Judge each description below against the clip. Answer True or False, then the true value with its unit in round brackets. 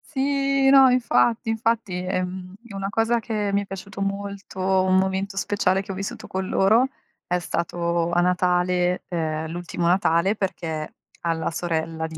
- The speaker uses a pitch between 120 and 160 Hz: False (190 Hz)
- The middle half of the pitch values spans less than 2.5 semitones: False (2.8 semitones)